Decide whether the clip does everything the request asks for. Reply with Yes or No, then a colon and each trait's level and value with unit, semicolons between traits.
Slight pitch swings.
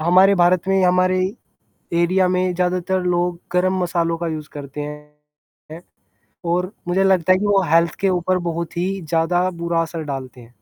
Yes: narrow, 1.9 semitones